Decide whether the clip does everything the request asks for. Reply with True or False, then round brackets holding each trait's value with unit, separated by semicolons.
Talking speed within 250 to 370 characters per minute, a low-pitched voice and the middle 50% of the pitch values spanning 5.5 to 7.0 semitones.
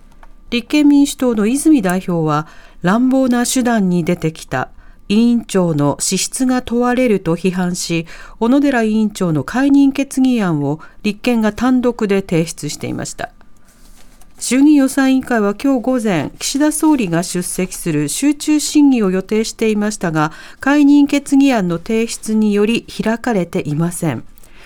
False (285 characters per minute; 220 Hz; 6.5 semitones)